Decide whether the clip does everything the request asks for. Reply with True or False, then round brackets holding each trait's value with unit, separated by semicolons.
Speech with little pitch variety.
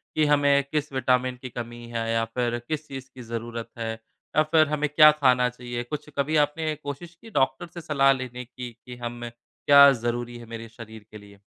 False (3.6 semitones)